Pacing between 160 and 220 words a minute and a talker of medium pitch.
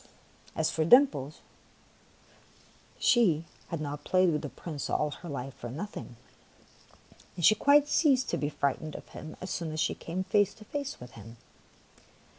Yes: average, 170 wpm; medium, 160 Hz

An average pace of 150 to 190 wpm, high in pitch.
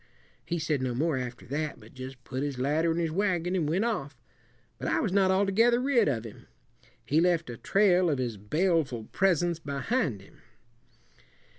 No: average, 180 wpm; medium, 160 Hz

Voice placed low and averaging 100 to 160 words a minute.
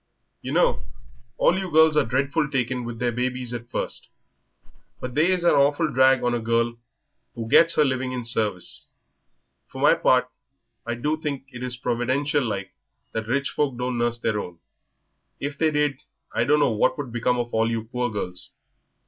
No: low, 125 Hz; average, 180 wpm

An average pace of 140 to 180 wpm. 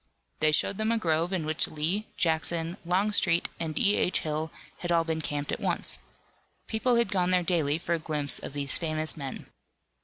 No: average, 190 wpm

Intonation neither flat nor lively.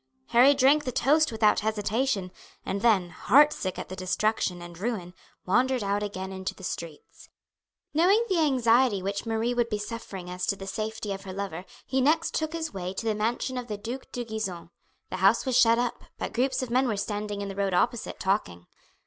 Yes: average, 4.6 semitones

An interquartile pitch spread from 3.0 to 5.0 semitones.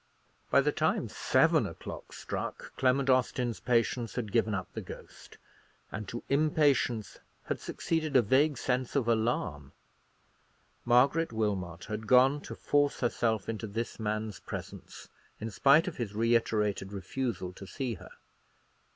Yes: average, 3.8 semitones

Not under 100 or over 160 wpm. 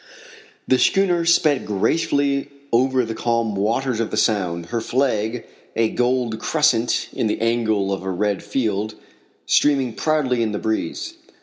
Yes: average, 145 wpm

